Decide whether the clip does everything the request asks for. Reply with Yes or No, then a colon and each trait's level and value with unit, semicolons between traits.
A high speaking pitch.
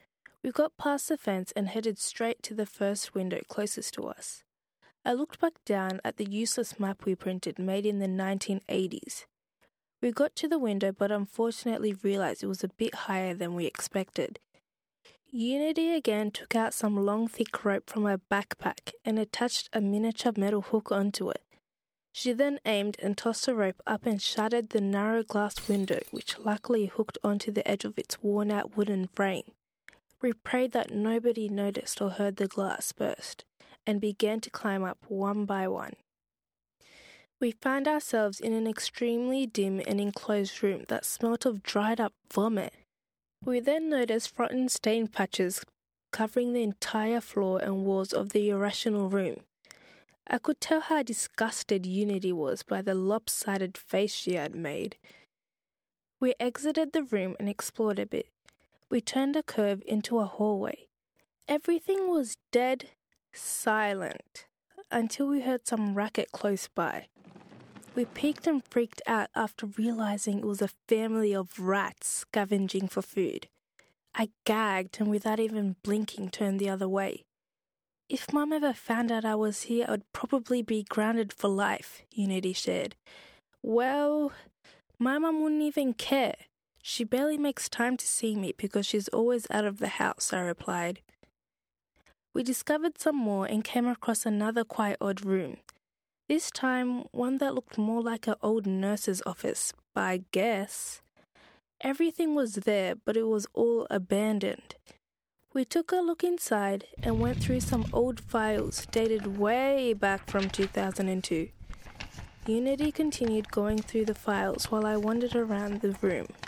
Yes: high, 215 Hz